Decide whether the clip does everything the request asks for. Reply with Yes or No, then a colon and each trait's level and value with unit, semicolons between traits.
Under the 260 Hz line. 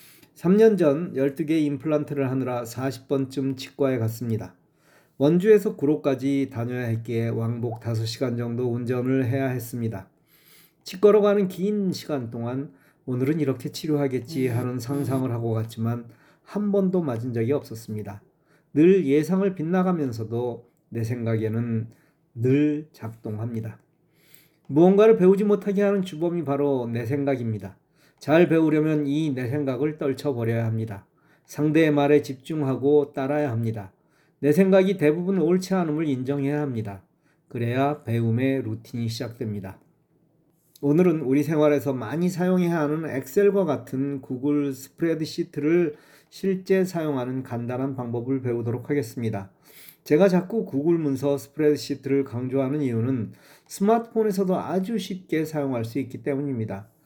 Yes: medium, 140 Hz